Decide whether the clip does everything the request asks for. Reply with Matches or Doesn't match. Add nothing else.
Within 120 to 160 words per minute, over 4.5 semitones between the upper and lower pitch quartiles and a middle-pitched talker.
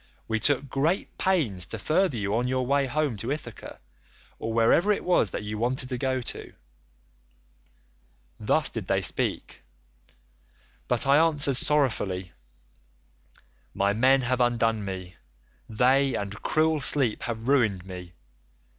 Doesn't match